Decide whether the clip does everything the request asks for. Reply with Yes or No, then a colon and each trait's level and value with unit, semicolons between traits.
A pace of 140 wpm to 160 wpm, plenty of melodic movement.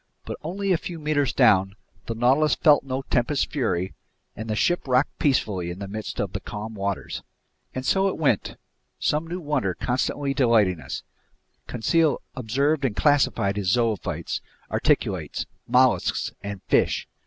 Yes: average, 155 wpm; wide, 6.1 semitones